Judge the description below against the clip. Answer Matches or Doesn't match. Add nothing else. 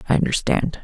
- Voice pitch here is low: Doesn't match